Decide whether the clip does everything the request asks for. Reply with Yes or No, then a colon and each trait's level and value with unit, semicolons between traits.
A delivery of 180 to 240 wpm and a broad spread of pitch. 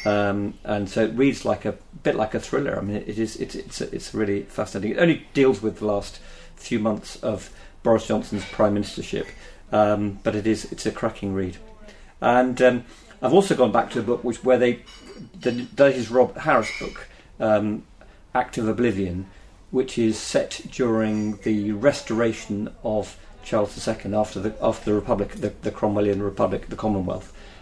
No: average, 185 wpm; average, 2.7 semitones